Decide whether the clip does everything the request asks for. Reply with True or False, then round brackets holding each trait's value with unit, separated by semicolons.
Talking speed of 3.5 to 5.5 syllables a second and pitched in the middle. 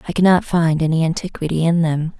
False (6.0 syllables/s; 165 Hz)